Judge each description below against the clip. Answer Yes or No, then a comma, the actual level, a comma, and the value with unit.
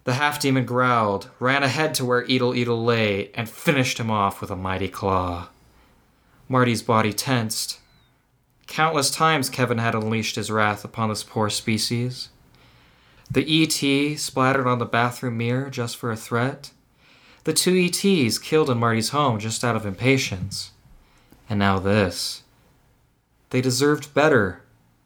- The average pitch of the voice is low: Yes, low, 125 Hz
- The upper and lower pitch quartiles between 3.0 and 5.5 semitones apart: Yes, average, 3.5 semitones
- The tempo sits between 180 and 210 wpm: No, average, 145 wpm